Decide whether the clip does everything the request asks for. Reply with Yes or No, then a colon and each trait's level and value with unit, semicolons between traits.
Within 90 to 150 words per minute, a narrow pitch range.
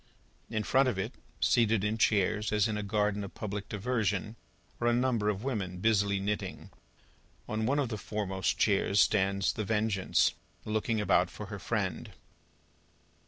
No: average, 165 wpm; narrow, 2.0 semitones